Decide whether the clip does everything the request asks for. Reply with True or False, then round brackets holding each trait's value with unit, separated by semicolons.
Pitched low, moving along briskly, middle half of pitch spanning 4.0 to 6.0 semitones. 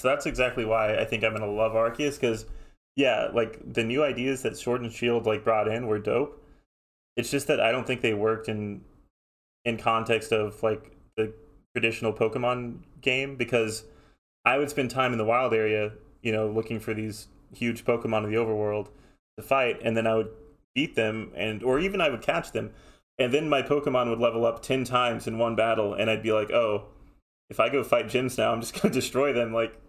False (115 Hz; 210 wpm; 2.5 semitones)